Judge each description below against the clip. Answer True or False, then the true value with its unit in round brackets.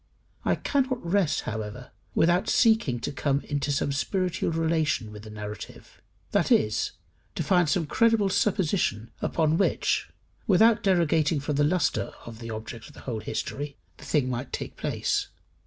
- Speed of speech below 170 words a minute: True (155 wpm)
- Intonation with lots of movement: True (7.0 semitones)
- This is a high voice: False (150 Hz)